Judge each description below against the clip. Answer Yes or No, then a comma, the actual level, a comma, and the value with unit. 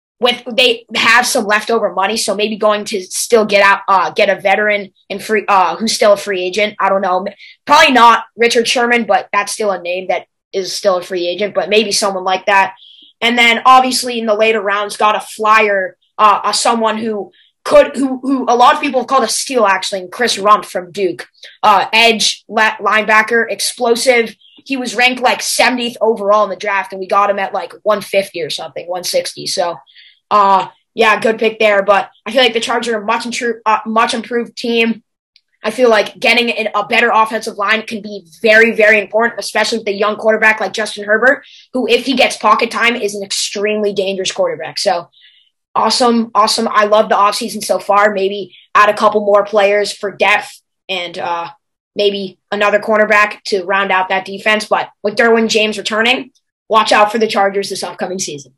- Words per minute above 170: Yes, average, 200 wpm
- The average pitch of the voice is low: No, high, 210 Hz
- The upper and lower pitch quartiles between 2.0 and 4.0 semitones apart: Yes, narrow, 2.6 semitones